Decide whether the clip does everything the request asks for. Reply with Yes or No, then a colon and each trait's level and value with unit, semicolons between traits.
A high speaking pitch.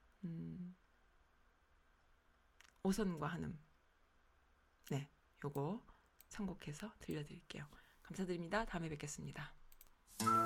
No: medium, 140 Hz